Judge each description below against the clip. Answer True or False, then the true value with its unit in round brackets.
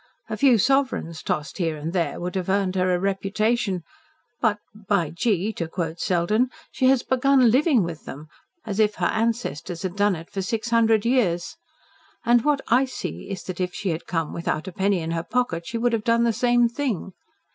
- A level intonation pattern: False (5.3 semitones)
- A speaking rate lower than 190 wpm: False (200 wpm)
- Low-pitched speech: False (200 Hz)